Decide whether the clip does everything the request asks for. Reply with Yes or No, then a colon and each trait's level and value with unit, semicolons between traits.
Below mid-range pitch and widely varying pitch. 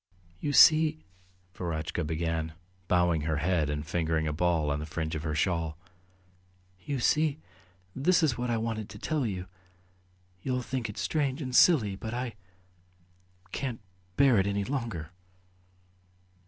Yes: low, 100 Hz; wide, 8.0 semitones